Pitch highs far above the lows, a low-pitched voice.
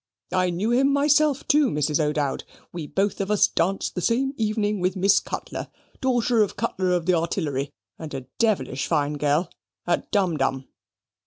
No: wide, 6.7 semitones; medium, 185 Hz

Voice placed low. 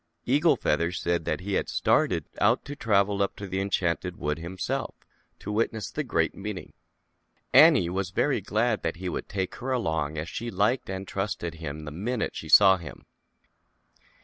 Yes: very low, 95 Hz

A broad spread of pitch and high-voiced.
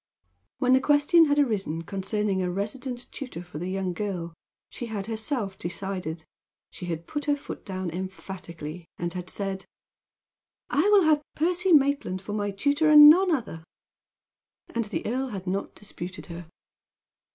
Yes: wide, 7.5 semitones; high, 200 Hz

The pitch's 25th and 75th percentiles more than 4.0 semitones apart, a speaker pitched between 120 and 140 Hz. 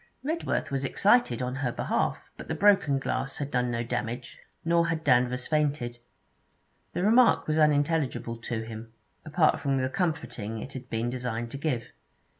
Yes: average, 4.6 semitones; low, 135 Hz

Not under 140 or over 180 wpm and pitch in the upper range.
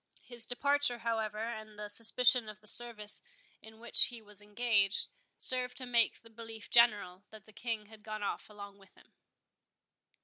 Yes: average, 170 wpm; high, 220 Hz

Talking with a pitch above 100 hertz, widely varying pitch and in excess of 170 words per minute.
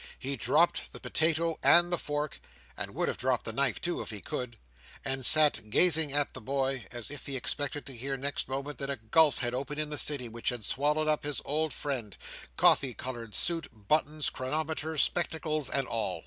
No: medium, 140 Hz; average, 3.8 semitones; average, 190 wpm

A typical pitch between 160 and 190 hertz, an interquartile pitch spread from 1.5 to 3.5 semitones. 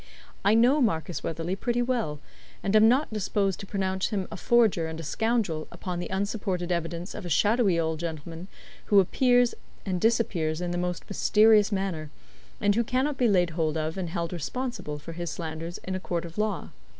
No: medium, 185 Hz; average, 4.6 semitones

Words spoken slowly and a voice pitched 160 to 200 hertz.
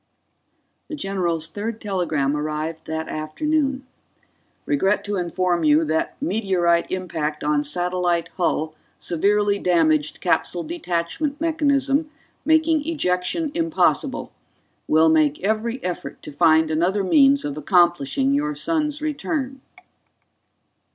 Yes: slow, 110 wpm; medium, 185 Hz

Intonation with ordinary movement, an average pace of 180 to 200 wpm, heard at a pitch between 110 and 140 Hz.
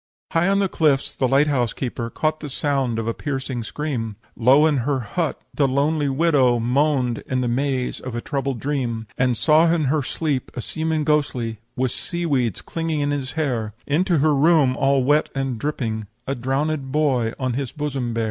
Yes: average, 3.4 semitones; average, 195 wpm; low, 135 Hz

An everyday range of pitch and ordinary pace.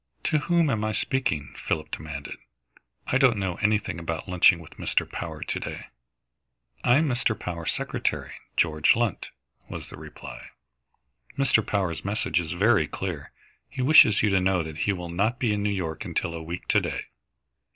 No: wide, 5.8 semitones; average, 175 wpm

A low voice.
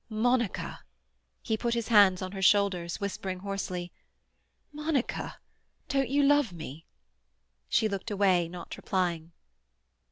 No: high, 200 Hz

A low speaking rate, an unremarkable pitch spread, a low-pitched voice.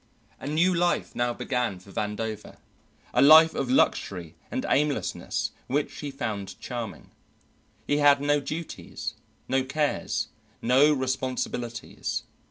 Yes: slow, 120 wpm; average, 3.8 semitones; low, 130 Hz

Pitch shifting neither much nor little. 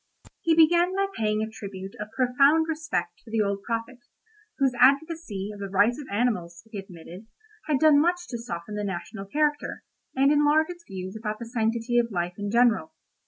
No: wide, 6.7 semitones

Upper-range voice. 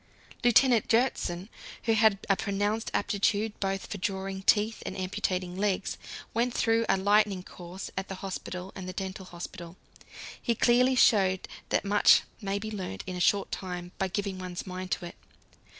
Yes: high, 195 Hz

